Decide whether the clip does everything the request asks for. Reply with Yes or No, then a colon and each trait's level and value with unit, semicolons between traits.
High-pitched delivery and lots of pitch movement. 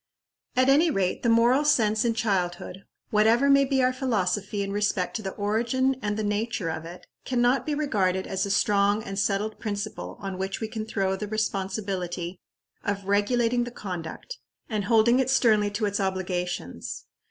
No: high, 210 Hz; average, 3.6 semitones